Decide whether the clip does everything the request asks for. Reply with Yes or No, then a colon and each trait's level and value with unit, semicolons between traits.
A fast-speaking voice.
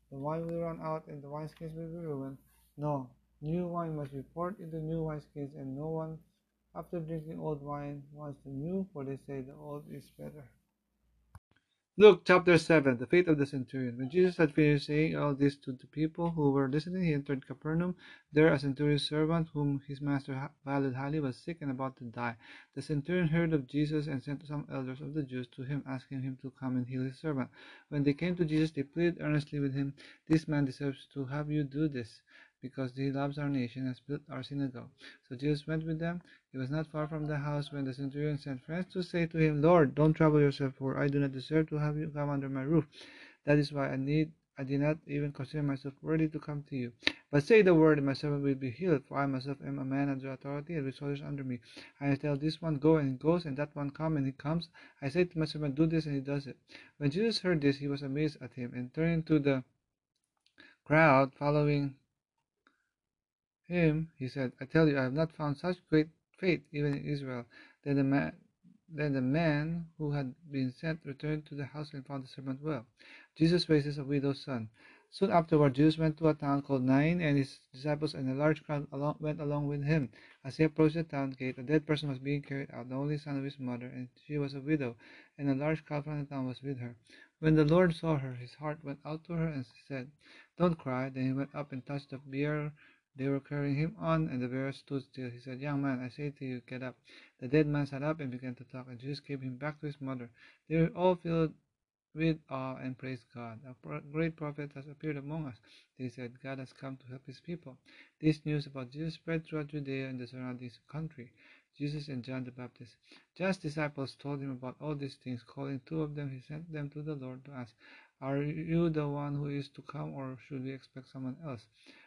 Yes: fast, 235 wpm